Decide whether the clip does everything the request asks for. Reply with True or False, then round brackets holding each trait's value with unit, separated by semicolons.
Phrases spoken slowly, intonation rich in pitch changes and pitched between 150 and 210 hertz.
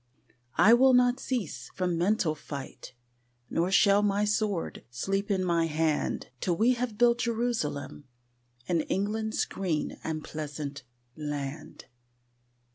True (120 wpm; 6.0 semitones; 190 Hz)